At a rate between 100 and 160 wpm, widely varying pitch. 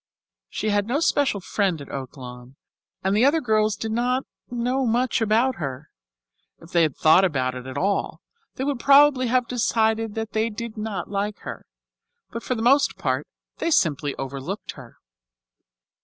No: average, 170 wpm; wide, 7.3 semitones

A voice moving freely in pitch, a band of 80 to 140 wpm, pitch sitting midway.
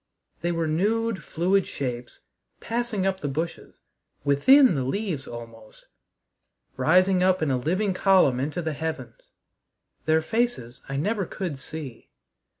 Yes: wide, 5.8 semitones; slow, 135 wpm; medium, 165 Hz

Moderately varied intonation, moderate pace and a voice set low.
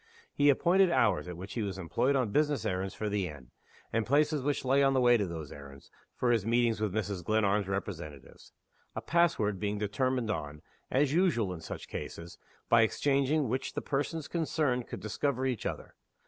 No: wide, 6.1 semitones; average, 190 wpm; low, 115 Hz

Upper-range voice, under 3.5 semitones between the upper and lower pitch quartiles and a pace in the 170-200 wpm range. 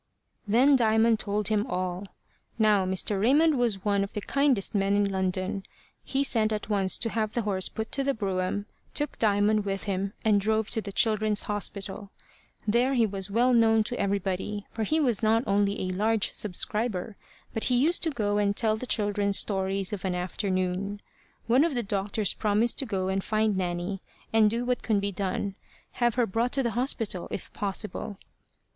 Yes: high, 210 Hz; narrow, 2.6 semitones; average, 190 wpm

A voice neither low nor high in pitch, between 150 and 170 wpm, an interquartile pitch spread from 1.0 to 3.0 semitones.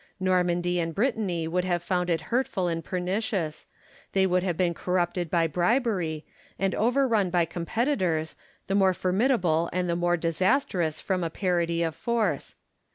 Yes: medium, 180 Hz; average, 155 wpm; narrow, 2.4 semitones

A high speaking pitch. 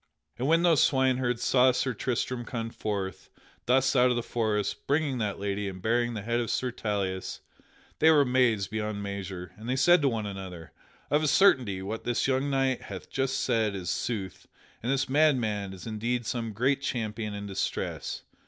No: low, 115 Hz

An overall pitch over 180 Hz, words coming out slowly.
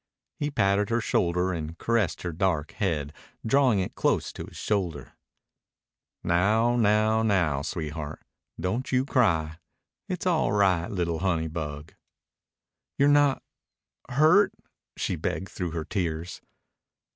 No: very low, 95 Hz; slow, 125 wpm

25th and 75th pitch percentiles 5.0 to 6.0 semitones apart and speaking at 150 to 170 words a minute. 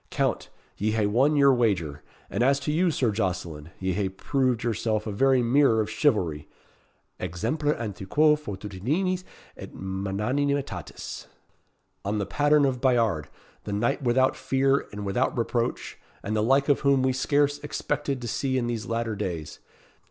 Yes: average, 5.3 semitones; average, 155 wpm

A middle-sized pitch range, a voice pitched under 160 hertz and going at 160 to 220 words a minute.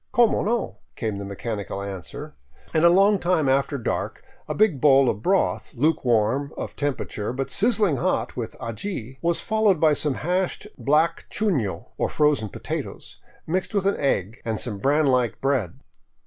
No: wide, 7.6 semitones; medium, 140 Hz; average, 175 wpm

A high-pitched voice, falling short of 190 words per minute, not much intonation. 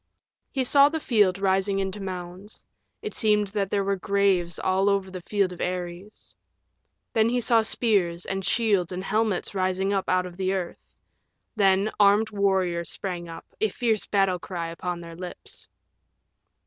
Yes: high, 195 Hz; average, 160 wpm; narrow, 2.3 semitones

